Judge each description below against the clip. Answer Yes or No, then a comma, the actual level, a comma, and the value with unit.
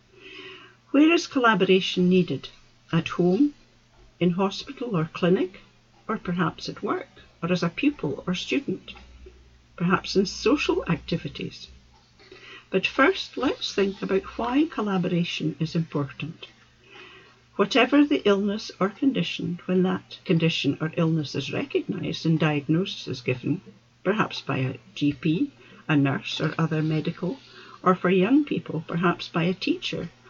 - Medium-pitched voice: Yes, medium, 175 Hz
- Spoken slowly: Yes, slow, 130 wpm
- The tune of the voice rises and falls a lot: No, average, 4.7 semitones